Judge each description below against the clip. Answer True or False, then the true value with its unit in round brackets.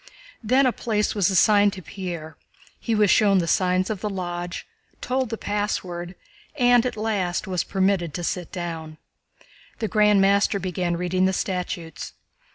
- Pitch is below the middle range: False (190 Hz)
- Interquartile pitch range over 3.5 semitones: False (3.1 semitones)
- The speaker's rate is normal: True (160 wpm)